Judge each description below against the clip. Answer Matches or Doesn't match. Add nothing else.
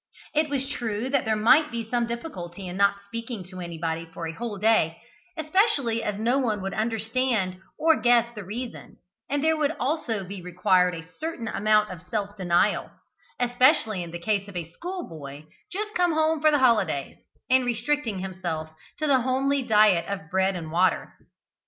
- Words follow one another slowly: Doesn't match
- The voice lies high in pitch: Matches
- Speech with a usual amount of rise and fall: Doesn't match